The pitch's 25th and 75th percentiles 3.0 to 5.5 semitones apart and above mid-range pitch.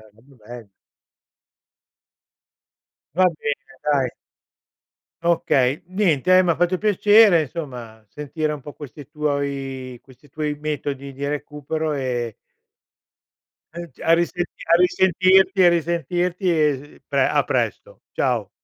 No: average, 4.2 semitones; medium, 150 Hz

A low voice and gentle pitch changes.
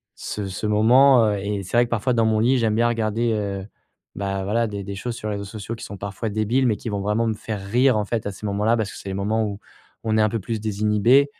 Yes: low, 110 Hz; narrow, 2.3 semitones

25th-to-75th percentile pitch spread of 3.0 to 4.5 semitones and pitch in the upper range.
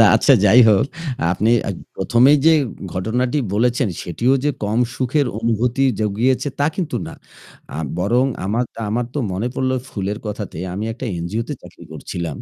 No: average, 3.7 semitones; low, 115 Hz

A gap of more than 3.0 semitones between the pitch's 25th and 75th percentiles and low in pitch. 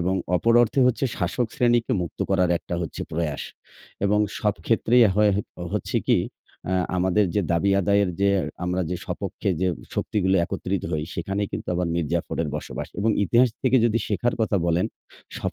Yes: average, 3.7 semitones; low, 100 Hz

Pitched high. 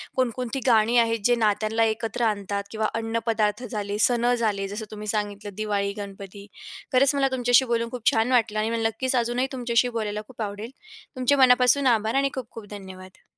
Yes: high, 225 Hz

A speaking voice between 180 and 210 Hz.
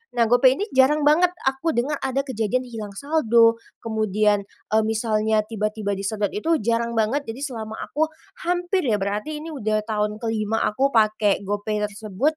No: high, 225 Hz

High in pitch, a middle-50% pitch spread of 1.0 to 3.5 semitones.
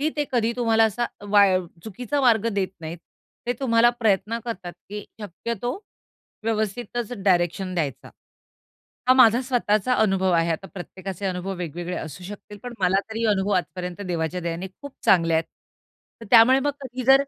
No: high, 205 Hz; average, 4.6 semitones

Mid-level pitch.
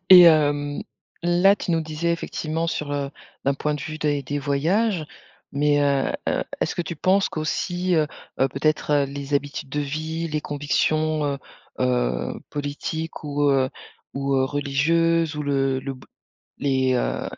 Yes: medium, 145 Hz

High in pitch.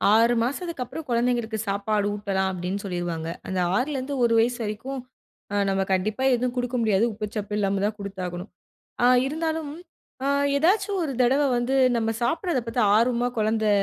Yes: high, 230 Hz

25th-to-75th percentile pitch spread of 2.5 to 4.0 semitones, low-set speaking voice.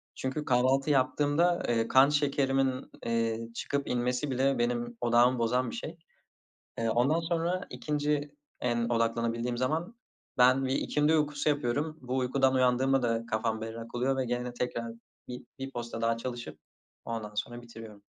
Yes: average, 3.0 semitones; low, 125 Hz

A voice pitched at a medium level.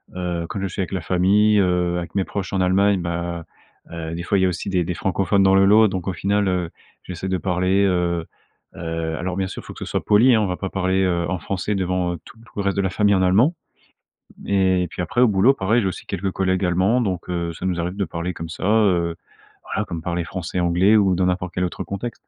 No: very low, 95 Hz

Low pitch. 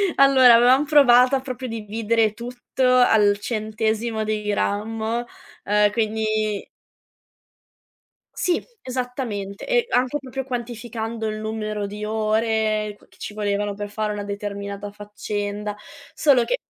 No: high, 220 Hz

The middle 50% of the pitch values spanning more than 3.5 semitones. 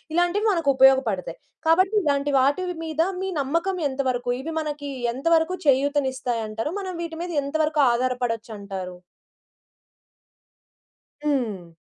Yes: average, 4.8 semitones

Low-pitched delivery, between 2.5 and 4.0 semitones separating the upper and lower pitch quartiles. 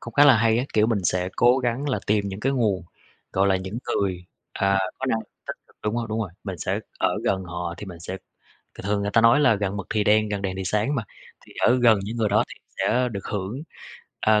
Yes: low, 105 Hz; average, 3.3 semitones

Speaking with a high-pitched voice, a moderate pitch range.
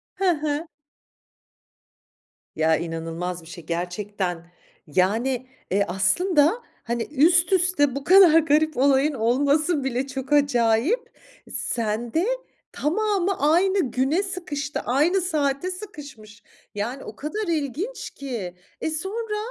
No: very high, 280 Hz; wide, 7.6 semitones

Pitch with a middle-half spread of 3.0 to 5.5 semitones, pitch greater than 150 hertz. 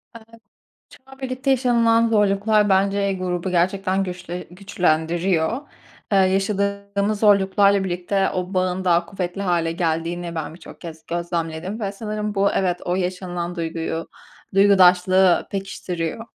No: narrow, 2.4 semitones; high, 190 Hz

